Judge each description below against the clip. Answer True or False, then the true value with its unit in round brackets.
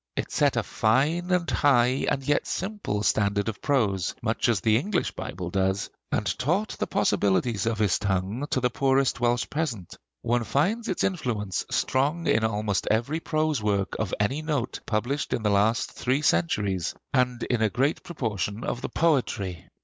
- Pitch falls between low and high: False (120 Hz)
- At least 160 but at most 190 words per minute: True (170 wpm)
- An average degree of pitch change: False (5.8 semitones)